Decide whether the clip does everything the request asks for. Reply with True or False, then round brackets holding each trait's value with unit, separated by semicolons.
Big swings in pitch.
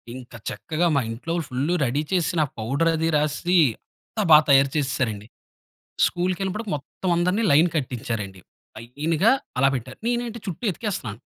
True (5.8 semitones)